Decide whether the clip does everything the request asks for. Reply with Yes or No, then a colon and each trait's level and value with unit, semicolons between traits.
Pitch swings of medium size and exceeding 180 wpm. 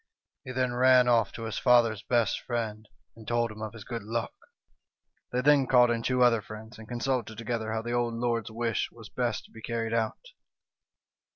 No: narrow, 1.7 semitones; average, 195 wpm